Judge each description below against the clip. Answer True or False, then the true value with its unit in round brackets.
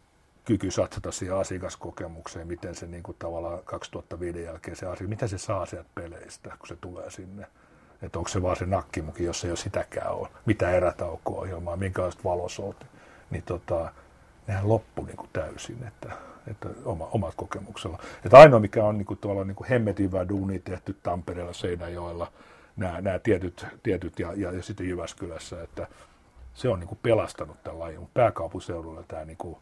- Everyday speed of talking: False (160 wpm)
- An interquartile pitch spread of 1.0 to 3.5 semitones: True (2.6 semitones)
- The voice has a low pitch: True (90 Hz)